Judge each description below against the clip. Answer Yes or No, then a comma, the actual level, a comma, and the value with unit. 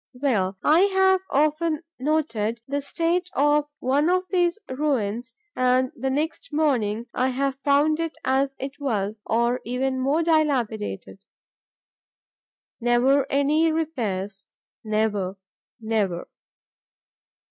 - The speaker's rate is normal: No, slow, 110 wpm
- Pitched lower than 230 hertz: No, very high, 270 Hz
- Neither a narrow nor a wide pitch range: Yes, average, 5.0 semitones